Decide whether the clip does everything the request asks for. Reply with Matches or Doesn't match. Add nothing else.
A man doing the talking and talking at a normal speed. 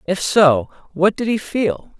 Matches